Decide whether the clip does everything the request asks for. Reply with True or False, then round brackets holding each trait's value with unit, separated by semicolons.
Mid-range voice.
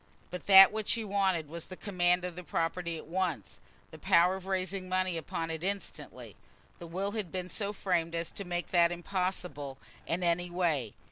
True (180 Hz)